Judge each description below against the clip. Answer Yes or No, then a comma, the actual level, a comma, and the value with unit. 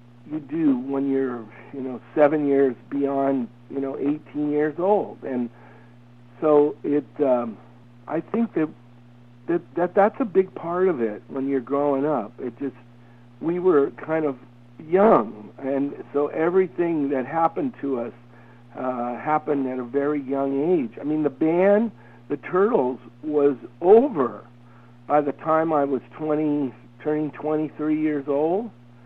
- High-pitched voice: No, medium, 140 Hz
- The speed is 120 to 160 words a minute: Yes, average, 150 wpm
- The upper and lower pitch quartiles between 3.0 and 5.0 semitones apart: Yes, average, 4.2 semitones